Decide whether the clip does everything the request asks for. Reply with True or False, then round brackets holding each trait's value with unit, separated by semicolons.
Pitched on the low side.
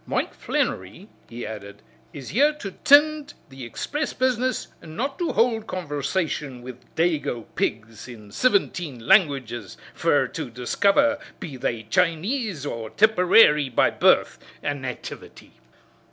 False (155 Hz)